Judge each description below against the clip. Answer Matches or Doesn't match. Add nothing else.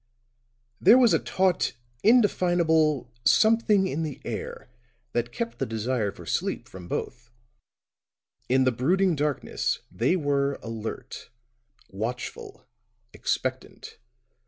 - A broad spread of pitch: Matches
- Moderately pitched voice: Matches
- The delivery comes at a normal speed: Doesn't match